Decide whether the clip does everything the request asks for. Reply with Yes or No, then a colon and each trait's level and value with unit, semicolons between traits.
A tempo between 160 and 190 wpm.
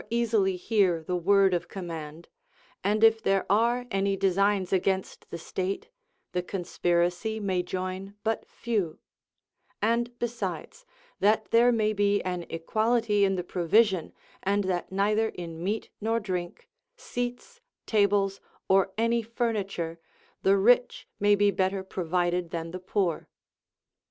No: slow, 135 wpm